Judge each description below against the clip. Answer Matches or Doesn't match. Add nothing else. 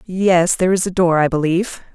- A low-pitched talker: Doesn't match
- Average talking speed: Doesn't match